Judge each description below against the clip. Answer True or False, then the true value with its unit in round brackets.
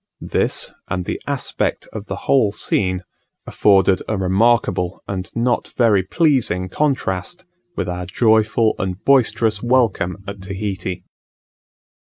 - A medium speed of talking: False (120 wpm)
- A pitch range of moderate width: True (4.0 semitones)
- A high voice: False (100 Hz)